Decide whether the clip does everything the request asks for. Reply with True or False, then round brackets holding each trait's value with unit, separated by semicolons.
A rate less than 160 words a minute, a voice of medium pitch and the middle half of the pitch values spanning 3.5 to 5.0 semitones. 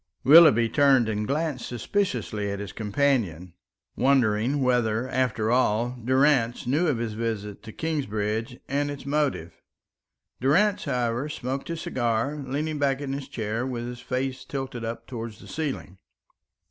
False (145 wpm; 125 Hz; 3.8 semitones)